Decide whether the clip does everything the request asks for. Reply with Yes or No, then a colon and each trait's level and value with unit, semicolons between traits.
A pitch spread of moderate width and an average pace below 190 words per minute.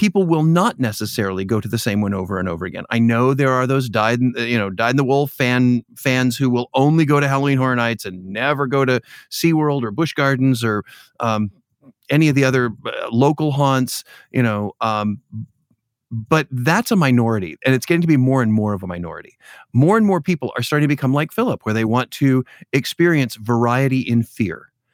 No: average, 3.9 semitones; fast, 205 wpm